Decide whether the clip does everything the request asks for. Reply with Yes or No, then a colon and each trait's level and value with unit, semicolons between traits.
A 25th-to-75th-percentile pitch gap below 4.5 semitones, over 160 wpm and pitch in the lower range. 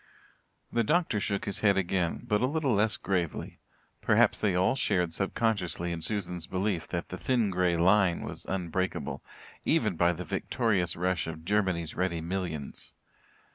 No: average, 3.3 semitones; average, 155 wpm; very low, 95 Hz